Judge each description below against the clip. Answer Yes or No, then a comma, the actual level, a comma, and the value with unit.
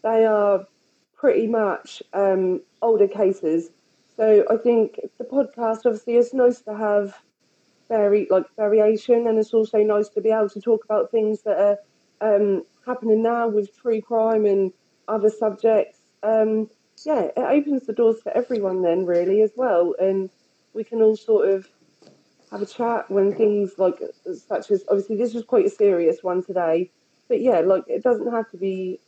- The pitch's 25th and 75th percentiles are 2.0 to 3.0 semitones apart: Yes, average, 2.7 semitones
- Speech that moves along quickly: No, average, 175 wpm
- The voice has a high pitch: Yes, high, 215 Hz